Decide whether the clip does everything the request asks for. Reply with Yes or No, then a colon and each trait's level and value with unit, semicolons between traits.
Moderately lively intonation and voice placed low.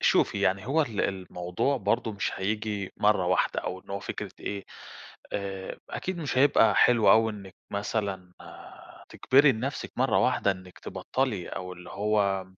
Yes: average, 3.3 semitones; low, 100 Hz